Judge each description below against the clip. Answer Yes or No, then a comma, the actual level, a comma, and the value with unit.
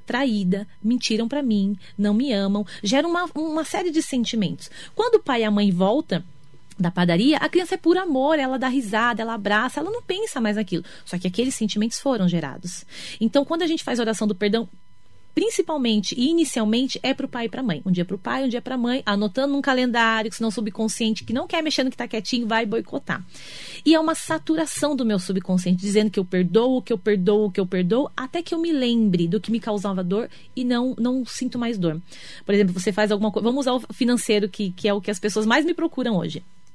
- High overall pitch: Yes, high, 230 Hz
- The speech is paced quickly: Yes, fast, 230 wpm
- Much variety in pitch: No, average, 4.7 semitones